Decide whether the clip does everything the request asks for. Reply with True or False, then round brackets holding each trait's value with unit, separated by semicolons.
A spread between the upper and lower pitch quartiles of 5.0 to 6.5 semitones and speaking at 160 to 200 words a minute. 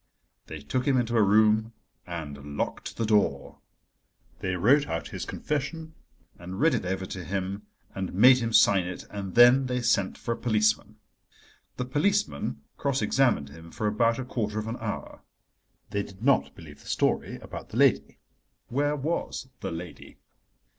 True (5.4 semitones; 165 wpm)